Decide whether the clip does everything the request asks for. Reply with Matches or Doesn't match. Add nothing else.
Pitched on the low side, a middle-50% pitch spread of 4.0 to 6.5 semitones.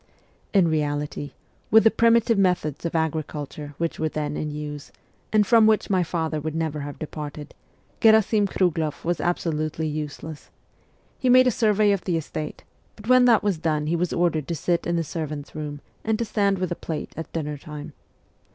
Doesn't match